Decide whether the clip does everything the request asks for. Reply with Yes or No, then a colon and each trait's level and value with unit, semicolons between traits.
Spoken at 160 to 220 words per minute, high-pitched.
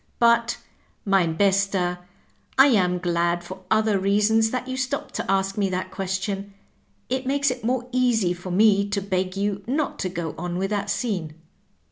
Yes: average, 170 wpm; high, 200 Hz